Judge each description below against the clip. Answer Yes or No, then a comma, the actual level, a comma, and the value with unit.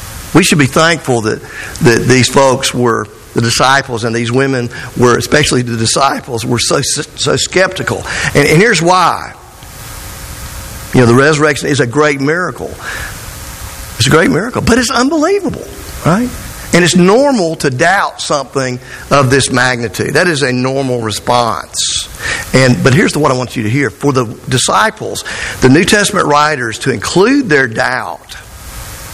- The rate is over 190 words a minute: No, average, 160 wpm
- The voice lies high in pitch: No, low, 130 Hz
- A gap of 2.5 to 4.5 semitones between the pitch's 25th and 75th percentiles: Yes, average, 3.9 semitones